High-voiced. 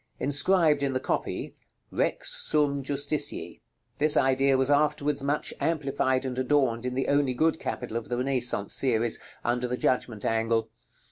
No: low, 135 Hz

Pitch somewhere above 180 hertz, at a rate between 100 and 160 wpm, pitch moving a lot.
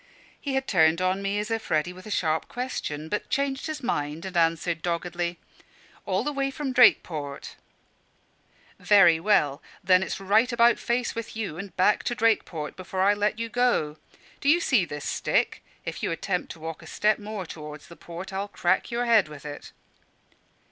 No: high, 190 Hz; average, 185 wpm; wide, 5.7 semitones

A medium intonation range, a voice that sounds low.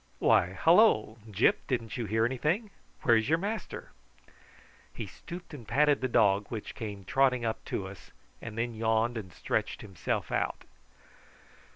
Yes: average, 4.3 semitones; low, 115 Hz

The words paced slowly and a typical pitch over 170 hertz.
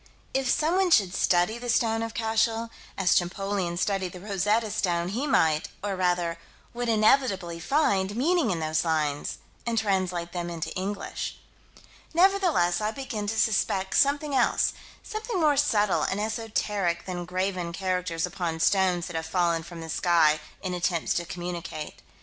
No: average, 155 wpm; high, 190 Hz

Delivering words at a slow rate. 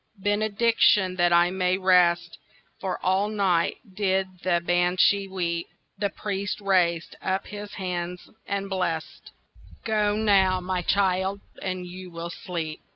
Yes: slow, 130 wpm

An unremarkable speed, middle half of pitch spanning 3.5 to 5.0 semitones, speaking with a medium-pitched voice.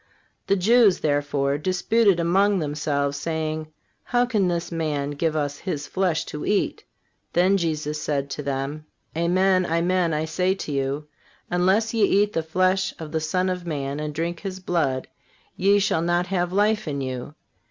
Yes: average, 165 wpm; average, 3.9 semitones; medium, 170 Hz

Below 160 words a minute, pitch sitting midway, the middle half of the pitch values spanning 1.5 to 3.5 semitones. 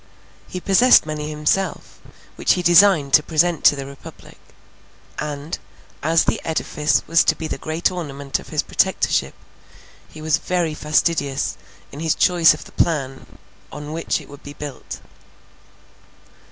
Yes: average, 150 wpm; medium, 155 Hz; narrow, 2.6 semitones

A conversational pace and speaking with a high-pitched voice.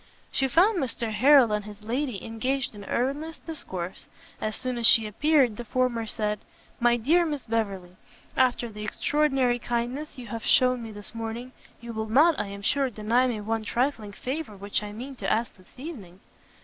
Yes: average, 185 wpm; high, 235 Hz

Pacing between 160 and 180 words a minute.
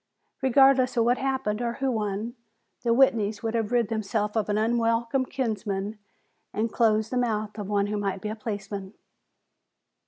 Yes: average, 165 wpm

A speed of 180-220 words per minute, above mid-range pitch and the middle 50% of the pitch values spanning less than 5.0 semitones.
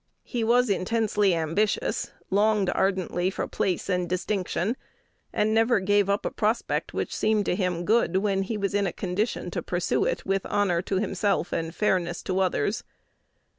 No: average, 170 wpm; high, 195 Hz; average, 2.7 semitones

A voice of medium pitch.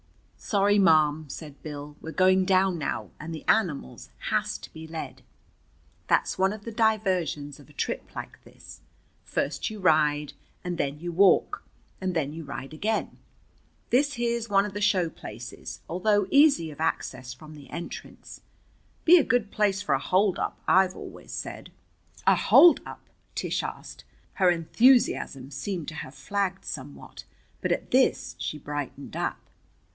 Yes: medium, 175 Hz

